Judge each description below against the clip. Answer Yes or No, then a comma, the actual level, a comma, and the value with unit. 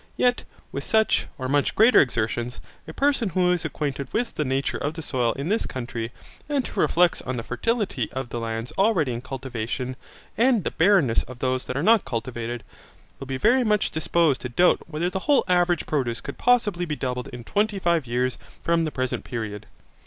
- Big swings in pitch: Yes, wide, 7.2 semitones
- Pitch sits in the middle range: Yes, medium, 145 Hz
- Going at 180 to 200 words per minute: Yes, average, 195 wpm